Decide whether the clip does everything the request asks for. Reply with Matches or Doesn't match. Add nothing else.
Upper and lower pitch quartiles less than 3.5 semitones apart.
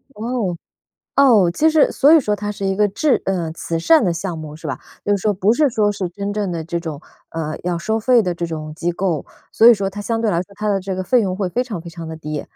Doesn't match